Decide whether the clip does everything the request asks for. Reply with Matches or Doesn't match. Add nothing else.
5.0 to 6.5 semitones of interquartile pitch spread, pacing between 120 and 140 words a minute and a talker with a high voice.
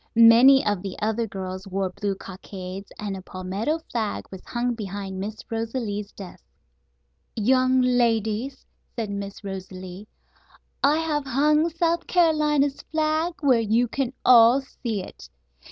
Matches